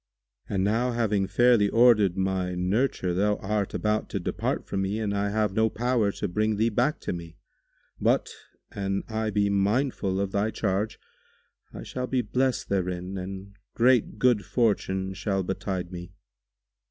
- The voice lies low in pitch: Yes, low, 100 Hz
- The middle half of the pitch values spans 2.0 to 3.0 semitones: Yes, narrow, 2.6 semitones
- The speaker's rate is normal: Yes, average, 160 wpm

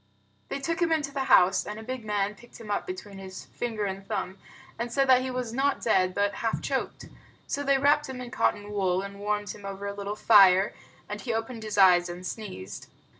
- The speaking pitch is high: Yes, high, 210 Hz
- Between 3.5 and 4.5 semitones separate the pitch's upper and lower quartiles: Yes, average, 4.2 semitones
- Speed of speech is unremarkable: No, fast, 220 wpm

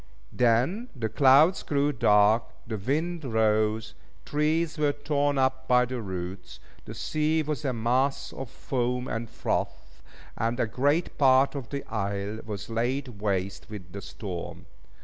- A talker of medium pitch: No, low, 125 Hz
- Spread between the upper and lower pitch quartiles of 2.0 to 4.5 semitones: No, average, 4.9 semitones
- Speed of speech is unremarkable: Yes, average, 150 wpm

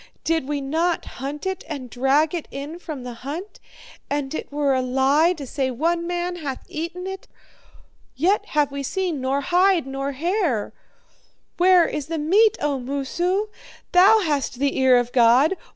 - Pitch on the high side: Yes, very high, 295 Hz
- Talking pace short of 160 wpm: No, average, 170 wpm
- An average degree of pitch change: Yes, average, 4.6 semitones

